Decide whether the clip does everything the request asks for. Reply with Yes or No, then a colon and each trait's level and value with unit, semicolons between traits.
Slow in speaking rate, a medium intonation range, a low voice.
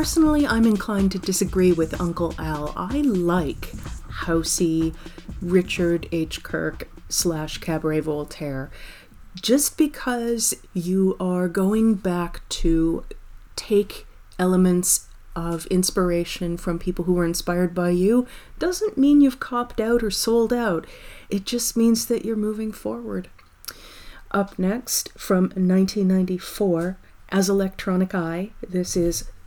No: slow, 120 wpm; average, 4.3 semitones; medium, 185 Hz